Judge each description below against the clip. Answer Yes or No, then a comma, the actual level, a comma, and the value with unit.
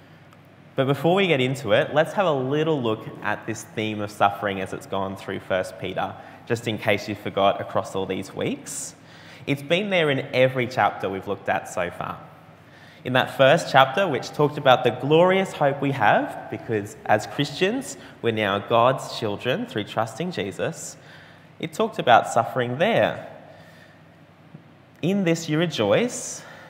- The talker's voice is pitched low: Yes, low, 130 Hz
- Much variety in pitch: Yes, wide, 6.8 semitones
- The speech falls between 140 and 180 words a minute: Yes, average, 165 wpm